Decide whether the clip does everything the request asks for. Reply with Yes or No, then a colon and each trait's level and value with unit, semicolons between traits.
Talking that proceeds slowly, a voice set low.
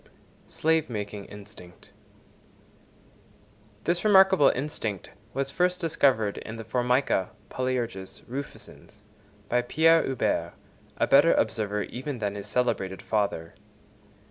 Yes: slow, 100 wpm; low, 120 Hz